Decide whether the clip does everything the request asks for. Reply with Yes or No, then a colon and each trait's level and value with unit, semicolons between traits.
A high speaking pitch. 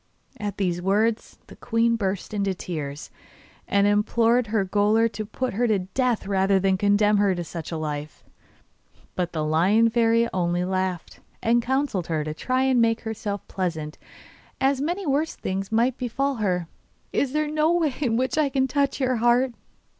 Yes: high, 215 Hz